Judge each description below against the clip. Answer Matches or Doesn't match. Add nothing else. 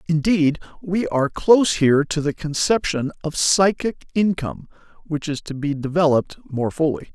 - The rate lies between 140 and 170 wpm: Matches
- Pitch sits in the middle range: Matches